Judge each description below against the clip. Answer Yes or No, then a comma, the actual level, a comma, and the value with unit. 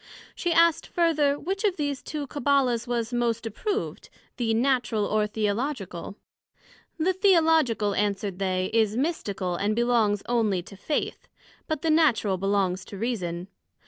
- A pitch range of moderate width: No, wide, 6.6 semitones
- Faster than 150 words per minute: No, average, 140 wpm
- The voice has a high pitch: Yes, high, 235 Hz